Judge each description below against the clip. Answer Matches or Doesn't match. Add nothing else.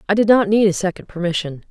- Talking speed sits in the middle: Doesn't match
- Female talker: Matches